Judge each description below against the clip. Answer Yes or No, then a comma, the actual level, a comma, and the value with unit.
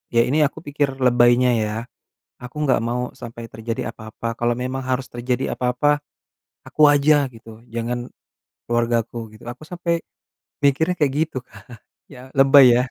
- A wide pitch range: No, average, 3.1 semitones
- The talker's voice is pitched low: Yes, low, 125 Hz